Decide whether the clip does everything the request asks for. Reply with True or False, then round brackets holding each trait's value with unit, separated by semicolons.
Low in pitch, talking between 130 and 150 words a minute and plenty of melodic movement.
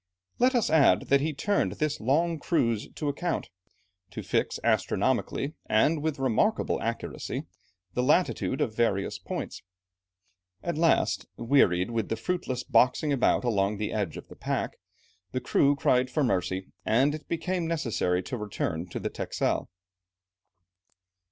True (130 Hz; 145 wpm; 6.3 semitones)